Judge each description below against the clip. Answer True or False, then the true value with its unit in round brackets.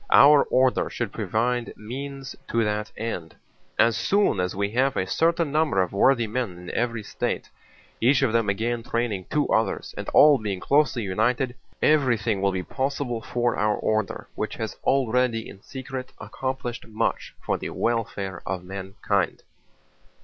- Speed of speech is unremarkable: True (155 wpm)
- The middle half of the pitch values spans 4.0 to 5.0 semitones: True (4.6 semitones)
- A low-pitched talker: True (115 Hz)